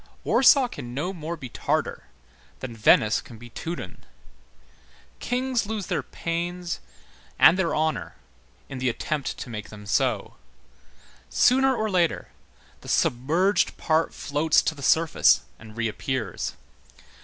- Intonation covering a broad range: Yes, wide, 6.9 semitones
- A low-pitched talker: No, medium, 155 Hz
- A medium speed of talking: No, slow, 130 wpm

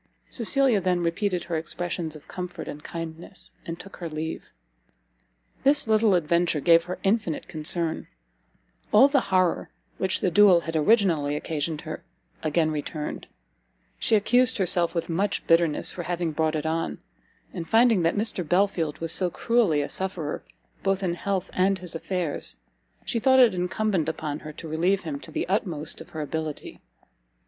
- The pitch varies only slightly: No, average, 3.6 semitones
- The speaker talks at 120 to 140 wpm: No, average, 165 wpm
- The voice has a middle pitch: Yes, medium, 175 Hz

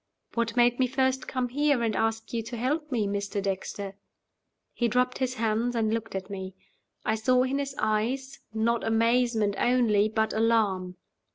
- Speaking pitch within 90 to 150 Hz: No, high, 230 Hz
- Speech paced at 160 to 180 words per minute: Yes, average, 170 wpm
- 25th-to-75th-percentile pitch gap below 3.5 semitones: Yes, average, 2.7 semitones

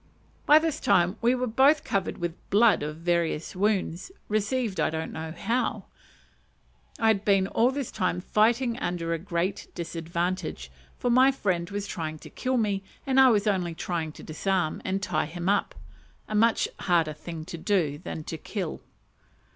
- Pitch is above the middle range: Yes, high, 195 Hz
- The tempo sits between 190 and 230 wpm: No, average, 165 wpm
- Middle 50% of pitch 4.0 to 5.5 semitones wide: Yes, average, 5.1 semitones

